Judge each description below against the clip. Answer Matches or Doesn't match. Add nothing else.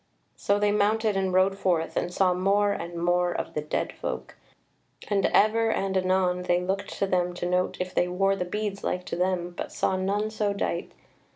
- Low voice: Doesn't match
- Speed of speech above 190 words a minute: Matches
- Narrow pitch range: Matches